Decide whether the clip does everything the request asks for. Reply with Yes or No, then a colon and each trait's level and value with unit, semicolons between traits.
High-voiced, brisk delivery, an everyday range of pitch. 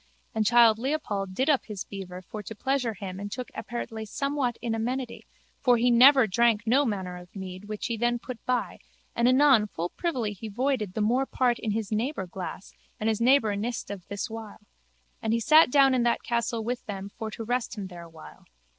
Yes: high, 225 Hz; fast, 210 wpm; average, 3.5 semitones